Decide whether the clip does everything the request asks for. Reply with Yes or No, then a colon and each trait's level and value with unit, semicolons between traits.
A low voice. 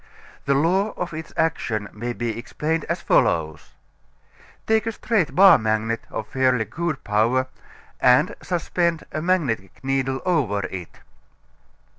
Yes: low, 130 Hz